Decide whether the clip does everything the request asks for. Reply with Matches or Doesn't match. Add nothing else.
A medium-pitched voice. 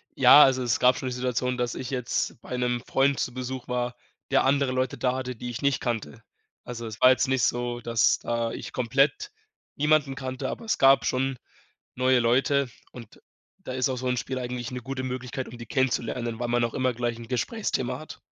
Doesn't match